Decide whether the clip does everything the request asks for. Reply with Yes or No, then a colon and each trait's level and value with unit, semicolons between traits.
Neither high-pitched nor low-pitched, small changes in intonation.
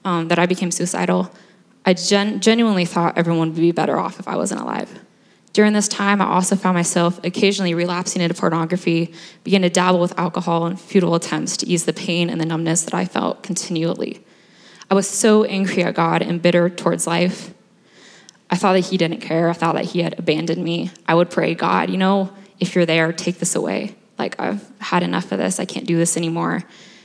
Yes: medium, 175 Hz; narrow, 2.3 semitones